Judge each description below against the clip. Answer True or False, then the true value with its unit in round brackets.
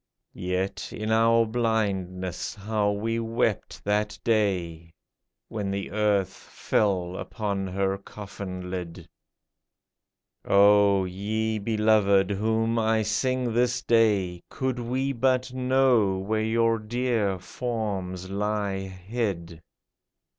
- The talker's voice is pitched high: False (105 Hz)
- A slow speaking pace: True (105 wpm)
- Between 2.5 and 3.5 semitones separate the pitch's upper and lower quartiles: True (2.9 semitones)